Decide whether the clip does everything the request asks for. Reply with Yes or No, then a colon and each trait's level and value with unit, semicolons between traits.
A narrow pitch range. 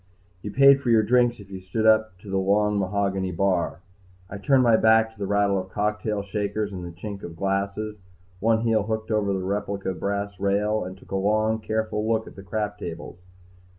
Yes: narrow, 1.9 semitones